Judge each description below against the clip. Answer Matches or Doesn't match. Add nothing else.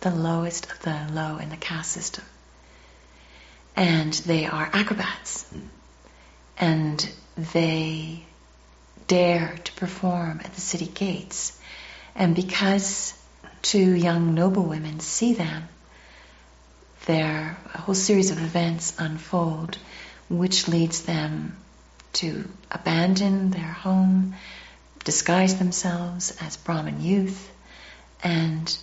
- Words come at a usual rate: Doesn't match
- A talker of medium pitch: Matches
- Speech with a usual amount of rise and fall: Matches